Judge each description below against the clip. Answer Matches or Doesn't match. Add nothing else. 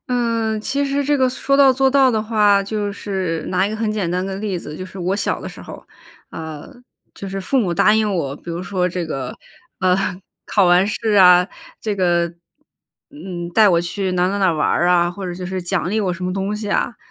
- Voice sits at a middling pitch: Doesn't match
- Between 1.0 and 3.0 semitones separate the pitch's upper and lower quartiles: Doesn't match